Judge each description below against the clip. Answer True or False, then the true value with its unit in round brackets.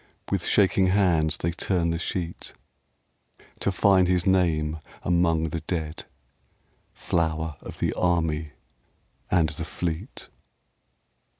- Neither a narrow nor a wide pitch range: False (2.3 semitones)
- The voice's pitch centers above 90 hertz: False (85 Hz)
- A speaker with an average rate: False (110 wpm)